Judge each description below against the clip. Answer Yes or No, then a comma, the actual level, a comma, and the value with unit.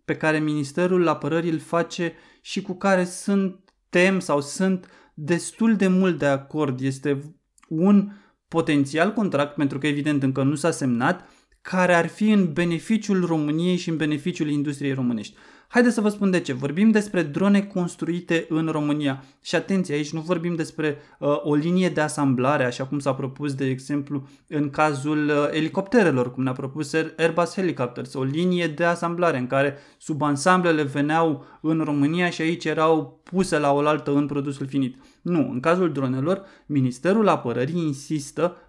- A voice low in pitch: No, medium, 155 Hz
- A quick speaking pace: No, average, 160 wpm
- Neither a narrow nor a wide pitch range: Yes, average, 3.6 semitones